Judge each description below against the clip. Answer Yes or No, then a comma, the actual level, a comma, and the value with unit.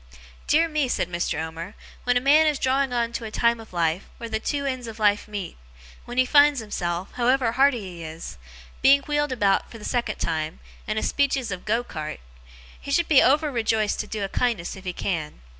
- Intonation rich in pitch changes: Yes, wide, 5.9 semitones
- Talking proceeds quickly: Yes, fast, 215 wpm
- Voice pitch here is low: No, high, 230 Hz